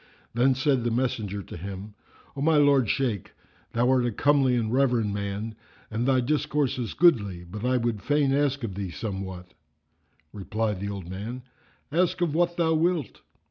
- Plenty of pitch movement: Yes, wide, 5.7 semitones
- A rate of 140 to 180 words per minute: Yes, average, 175 wpm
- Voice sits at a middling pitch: No, low, 120 Hz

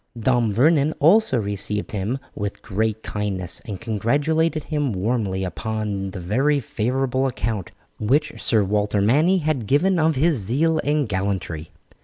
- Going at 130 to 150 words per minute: Yes, average, 140 wpm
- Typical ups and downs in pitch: No, wide, 6.3 semitones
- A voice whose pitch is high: No, low, 115 Hz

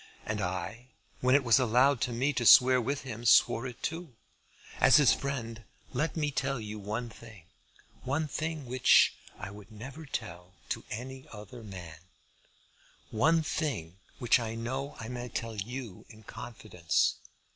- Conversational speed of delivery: Yes, average, 155 wpm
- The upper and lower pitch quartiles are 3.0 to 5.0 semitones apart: Yes, average, 3.7 semitones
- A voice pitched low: Yes, low, 120 Hz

